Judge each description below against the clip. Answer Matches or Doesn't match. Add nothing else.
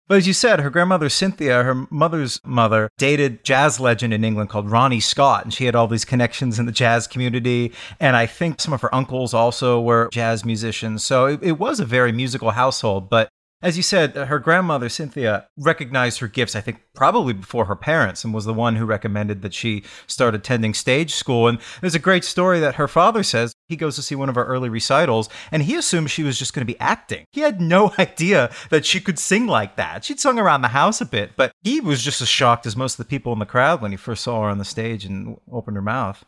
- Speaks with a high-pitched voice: Doesn't match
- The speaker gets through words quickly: Matches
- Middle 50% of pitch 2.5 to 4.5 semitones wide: Doesn't match